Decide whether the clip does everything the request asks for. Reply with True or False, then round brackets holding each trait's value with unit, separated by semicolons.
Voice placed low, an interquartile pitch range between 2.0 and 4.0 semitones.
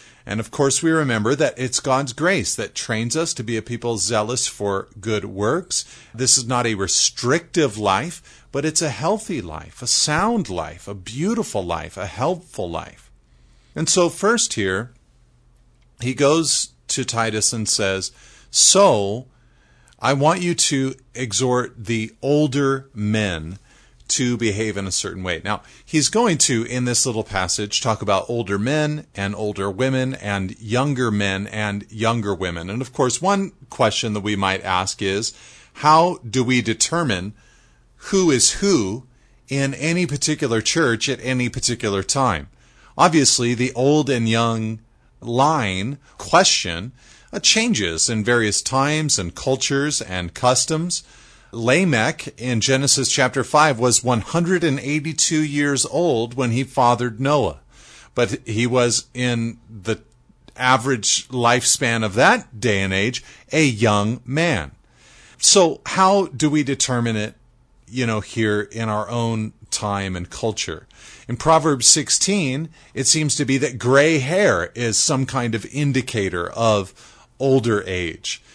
False (120 Hz; 4.8 semitones)